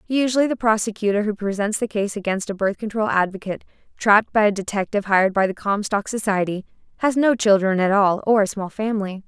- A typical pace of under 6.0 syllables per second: No, 6.2 syllables/s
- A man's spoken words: No, female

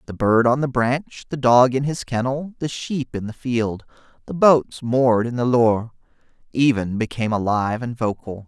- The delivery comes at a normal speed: Yes, average, 185 wpm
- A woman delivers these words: No, male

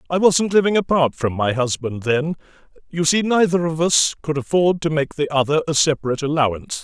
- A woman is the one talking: No, male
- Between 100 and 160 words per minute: No, average, 195 wpm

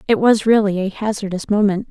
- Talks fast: No, average, 190 wpm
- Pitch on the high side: Yes, high, 205 Hz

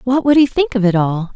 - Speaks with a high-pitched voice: Yes, high, 235 Hz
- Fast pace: Yes, fast, 310 wpm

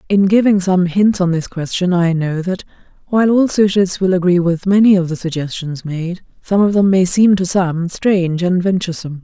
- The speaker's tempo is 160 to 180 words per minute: No, average, 200 wpm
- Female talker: Yes, female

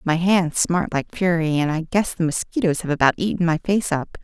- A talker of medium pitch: Yes, medium, 170 Hz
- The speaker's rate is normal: No, fast, 225 wpm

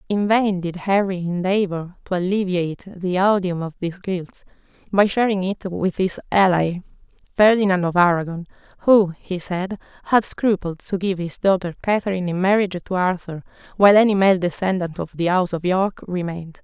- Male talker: No, female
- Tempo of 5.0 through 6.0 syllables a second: Yes, 5.3 syllables/s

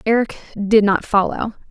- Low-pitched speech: No, high, 210 Hz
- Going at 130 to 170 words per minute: Yes, average, 140 wpm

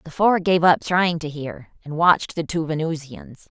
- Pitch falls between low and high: Yes, medium, 160 Hz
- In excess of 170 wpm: Yes, average, 200 wpm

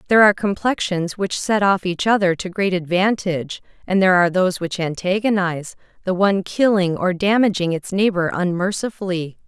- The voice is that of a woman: Yes, female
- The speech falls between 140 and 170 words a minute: Yes, average, 160 wpm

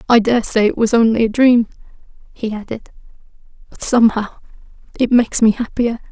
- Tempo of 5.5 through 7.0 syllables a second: Yes, 5.7 syllables/s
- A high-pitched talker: Yes, high, 230 Hz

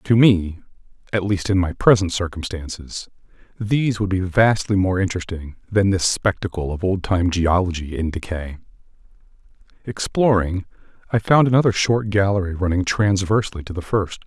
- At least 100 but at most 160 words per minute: Yes, average, 140 wpm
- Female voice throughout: No, male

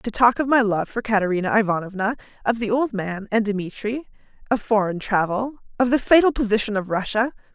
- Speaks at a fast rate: No, average, 185 wpm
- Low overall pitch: No, high, 220 Hz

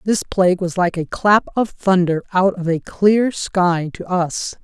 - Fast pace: No, average, 195 wpm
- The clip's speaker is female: Yes, female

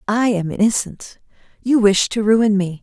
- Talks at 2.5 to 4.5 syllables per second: Yes, 4.4 syllables/s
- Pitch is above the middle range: Yes, high, 210 Hz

